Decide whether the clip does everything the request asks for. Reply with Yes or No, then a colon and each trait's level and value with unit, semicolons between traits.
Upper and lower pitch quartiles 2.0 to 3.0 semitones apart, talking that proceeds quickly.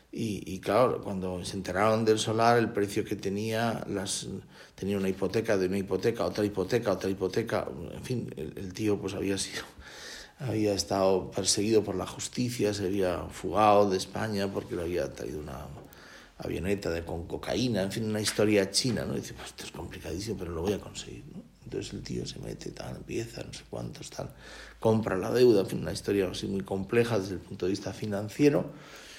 Yes: narrow, 2.4 semitones; fast, 195 wpm